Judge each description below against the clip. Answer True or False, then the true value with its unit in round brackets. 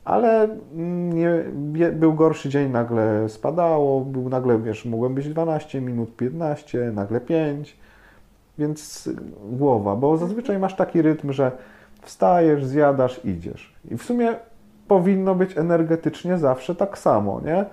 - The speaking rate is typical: True (130 wpm)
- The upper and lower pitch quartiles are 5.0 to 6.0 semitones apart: True (5.4 semitones)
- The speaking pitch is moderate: True (150 Hz)